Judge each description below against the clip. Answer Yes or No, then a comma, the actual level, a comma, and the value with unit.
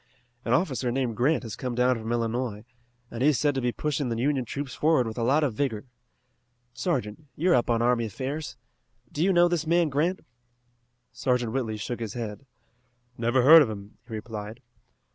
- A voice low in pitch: Yes, low, 125 Hz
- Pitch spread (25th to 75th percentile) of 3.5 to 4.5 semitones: Yes, average, 4.0 semitones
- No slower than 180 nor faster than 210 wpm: Yes, average, 195 wpm